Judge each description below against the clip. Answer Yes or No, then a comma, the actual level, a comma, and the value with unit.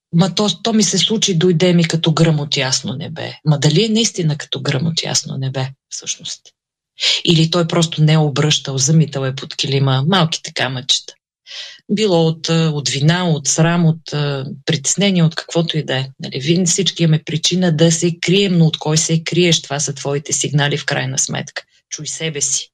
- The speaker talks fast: Yes, fast, 195 wpm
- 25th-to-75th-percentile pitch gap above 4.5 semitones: No, average, 3.3 semitones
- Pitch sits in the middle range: Yes, medium, 160 Hz